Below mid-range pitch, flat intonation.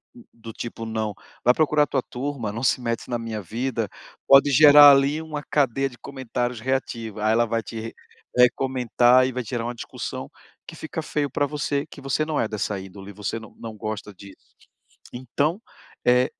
No: low, 125 Hz; average, 3.8 semitones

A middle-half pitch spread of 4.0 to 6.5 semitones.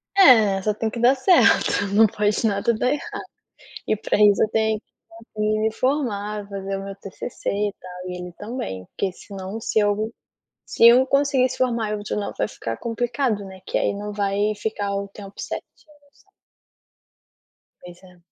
No: narrow, 2.5 semitones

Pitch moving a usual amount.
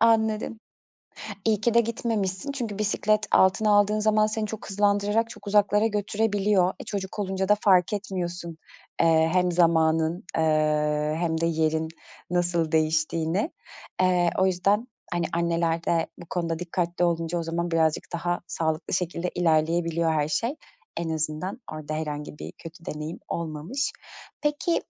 Yes: average, 4.2 semitones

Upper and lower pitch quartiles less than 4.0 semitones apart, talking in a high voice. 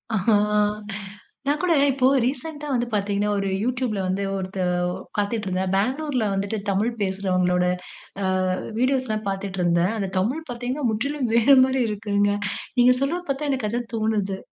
No: average, 4.6 semitones; high, 215 Hz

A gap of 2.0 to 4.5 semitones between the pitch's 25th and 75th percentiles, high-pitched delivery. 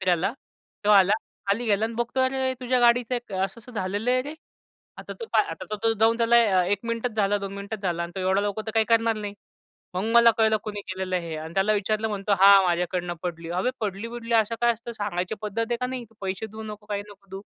Yes: average, 3.2 semitones; high, 210 Hz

